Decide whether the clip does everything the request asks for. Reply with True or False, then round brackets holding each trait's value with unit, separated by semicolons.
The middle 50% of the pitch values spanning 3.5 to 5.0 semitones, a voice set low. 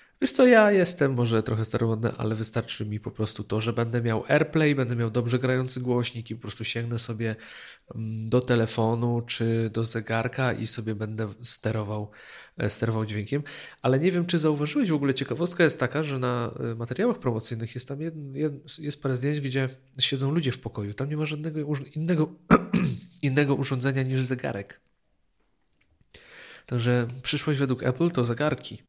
True (4.5 semitones; 125 Hz)